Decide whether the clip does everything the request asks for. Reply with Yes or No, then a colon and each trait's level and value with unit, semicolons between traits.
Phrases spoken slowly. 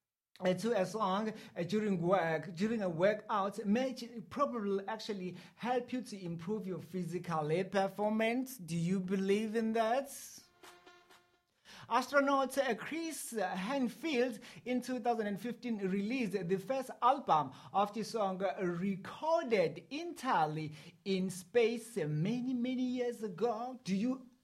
Yes: slow, 110 wpm